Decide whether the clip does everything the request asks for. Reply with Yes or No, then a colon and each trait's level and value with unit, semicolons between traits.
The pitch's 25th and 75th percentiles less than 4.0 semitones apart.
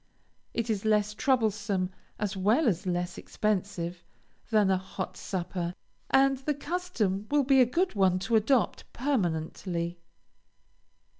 No: average, 5.3 semitones